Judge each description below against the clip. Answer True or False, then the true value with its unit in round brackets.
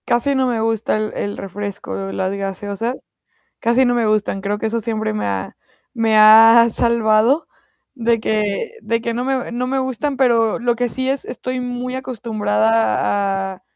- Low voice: False (225 Hz)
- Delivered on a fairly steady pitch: False (3.1 semitones)